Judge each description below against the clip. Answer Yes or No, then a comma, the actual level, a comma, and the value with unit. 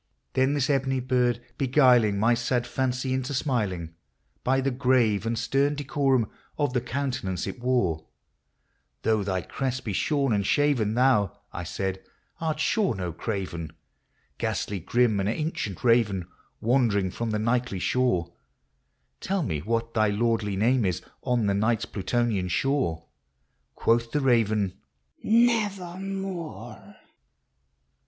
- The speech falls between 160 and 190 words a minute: No, average, 140 wpm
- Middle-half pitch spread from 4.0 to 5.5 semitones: Yes, average, 4.8 semitones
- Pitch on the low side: Yes, low, 120 Hz